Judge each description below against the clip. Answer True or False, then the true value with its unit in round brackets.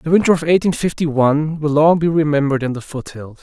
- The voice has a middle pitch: True (150 Hz)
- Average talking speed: False (230 wpm)